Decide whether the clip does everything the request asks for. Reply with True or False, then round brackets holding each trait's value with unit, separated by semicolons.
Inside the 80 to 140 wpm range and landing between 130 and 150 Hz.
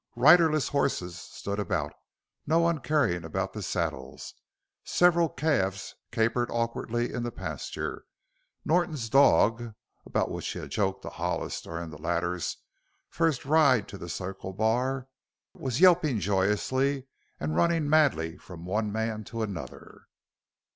False (135 wpm; 115 Hz)